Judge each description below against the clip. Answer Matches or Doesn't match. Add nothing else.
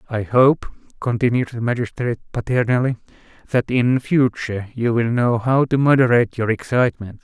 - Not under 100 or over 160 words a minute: Matches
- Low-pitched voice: Matches